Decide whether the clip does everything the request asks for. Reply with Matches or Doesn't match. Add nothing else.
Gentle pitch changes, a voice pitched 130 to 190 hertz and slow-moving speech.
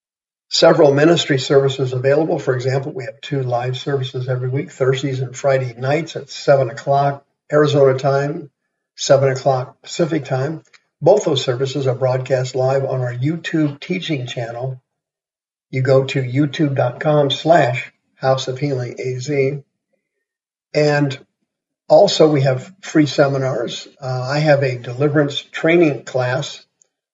Matches